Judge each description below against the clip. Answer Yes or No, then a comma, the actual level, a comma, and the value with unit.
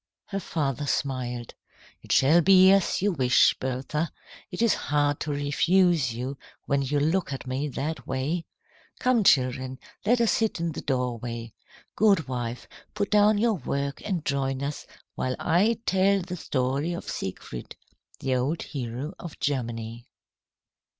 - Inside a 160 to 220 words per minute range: No, average, 145 wpm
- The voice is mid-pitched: Yes, medium, 145 Hz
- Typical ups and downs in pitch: No, wide, 5.8 semitones